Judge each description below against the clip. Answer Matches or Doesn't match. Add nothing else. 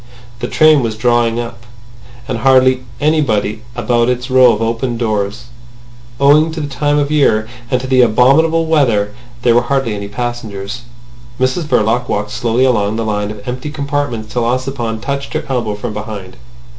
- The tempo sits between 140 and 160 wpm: Doesn't match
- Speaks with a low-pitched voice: Matches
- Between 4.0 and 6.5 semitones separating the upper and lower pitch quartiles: Doesn't match